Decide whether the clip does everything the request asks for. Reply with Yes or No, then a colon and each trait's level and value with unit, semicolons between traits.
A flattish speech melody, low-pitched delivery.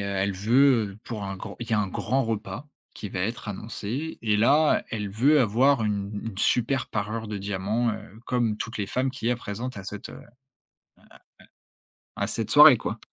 No: average, 3.2 semitones; low, 110 Hz